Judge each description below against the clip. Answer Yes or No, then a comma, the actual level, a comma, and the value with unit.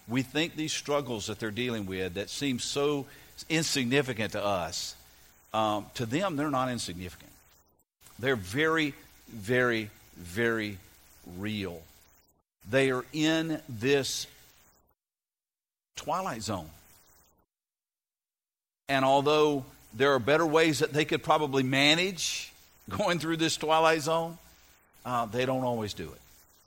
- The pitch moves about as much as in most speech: No, wide, 7.8 semitones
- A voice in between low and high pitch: No, low, 125 Hz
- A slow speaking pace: Yes, slow, 120 wpm